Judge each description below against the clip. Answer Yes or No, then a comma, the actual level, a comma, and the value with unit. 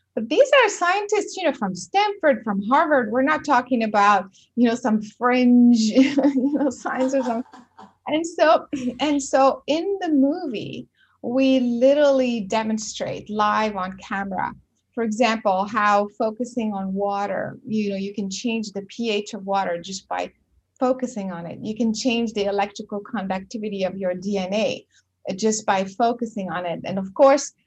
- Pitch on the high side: Yes, high, 230 Hz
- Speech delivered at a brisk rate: No, average, 160 wpm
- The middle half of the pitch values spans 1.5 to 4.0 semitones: No, average, 5.1 semitones